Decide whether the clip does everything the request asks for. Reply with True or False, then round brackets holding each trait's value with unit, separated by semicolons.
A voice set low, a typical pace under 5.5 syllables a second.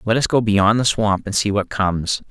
True (105 Hz; 5.2 syllables/s)